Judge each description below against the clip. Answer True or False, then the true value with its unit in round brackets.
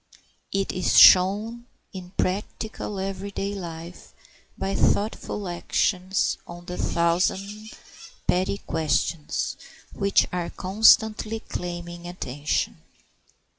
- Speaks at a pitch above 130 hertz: True (185 Hz)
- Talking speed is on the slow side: True (95 wpm)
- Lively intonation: False (2.6 semitones)